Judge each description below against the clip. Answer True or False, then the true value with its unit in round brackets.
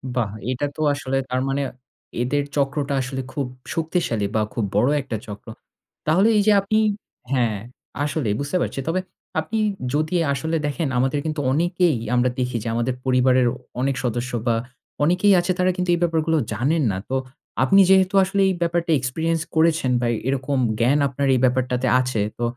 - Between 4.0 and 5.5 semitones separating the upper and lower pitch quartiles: True (4.6 semitones)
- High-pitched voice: False (140 Hz)